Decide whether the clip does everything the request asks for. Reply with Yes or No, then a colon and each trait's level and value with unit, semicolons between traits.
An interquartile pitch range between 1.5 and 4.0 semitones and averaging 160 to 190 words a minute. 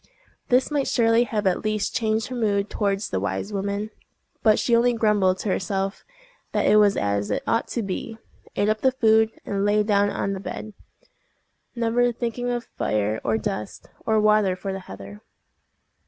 Yes: average, 2.9 semitones; average, 180 wpm